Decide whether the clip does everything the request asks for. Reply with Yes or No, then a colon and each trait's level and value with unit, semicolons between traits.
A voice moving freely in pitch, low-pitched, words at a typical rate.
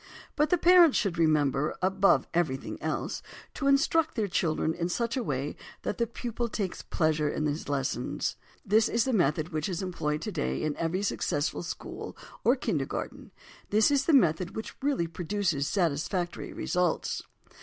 No: wide, 6.7 semitones; medium, 180 Hz; average, 160 wpm